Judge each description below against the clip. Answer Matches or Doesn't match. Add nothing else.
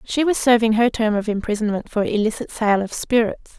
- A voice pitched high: Matches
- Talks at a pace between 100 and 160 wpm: Doesn't match